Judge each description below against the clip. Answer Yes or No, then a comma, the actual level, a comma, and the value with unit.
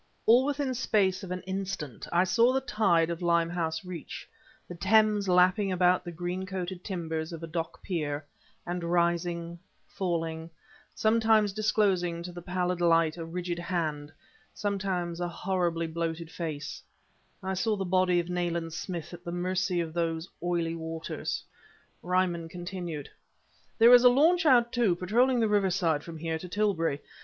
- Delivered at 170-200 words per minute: No, average, 155 wpm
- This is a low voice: No, medium, 175 Hz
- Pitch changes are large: No, narrow, 2.5 semitones